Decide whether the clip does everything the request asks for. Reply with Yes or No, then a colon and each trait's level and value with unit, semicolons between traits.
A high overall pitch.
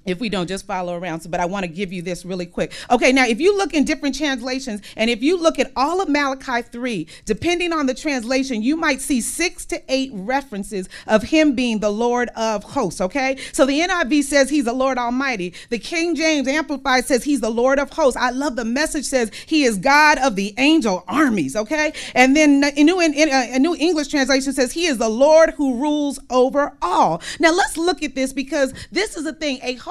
Yes: very high, 270 Hz